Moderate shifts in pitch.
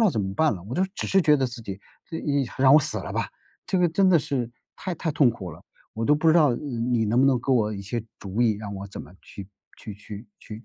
No: wide, 6.0 semitones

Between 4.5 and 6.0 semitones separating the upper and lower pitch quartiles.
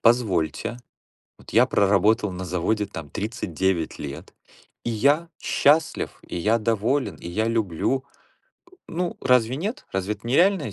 Yes: wide, 5.6 semitones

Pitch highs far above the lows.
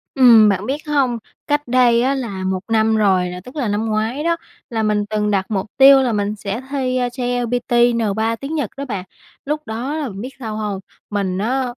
No: average, 3.8 semitones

